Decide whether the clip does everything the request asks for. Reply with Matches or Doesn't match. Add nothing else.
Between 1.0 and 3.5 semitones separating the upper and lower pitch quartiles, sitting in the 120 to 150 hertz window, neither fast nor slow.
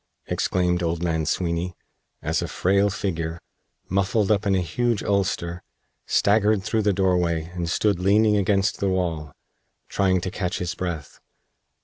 Doesn't match